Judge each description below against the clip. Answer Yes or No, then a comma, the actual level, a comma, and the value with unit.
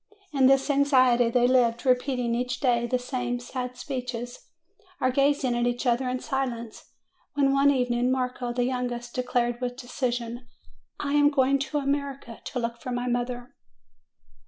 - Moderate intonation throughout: No, narrow, 1.6 semitones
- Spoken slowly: No, average, 160 wpm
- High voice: Yes, very high, 250 Hz